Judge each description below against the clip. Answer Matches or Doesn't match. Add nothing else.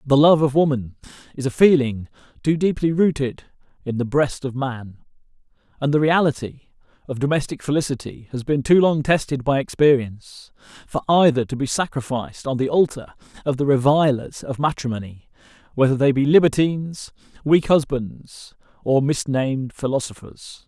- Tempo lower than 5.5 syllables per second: Matches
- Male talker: Matches